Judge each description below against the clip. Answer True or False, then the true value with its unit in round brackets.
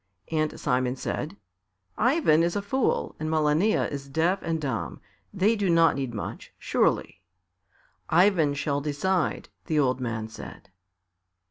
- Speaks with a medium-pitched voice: True (155 Hz)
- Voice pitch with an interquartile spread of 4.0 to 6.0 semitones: True (5.0 semitones)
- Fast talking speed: False (135 wpm)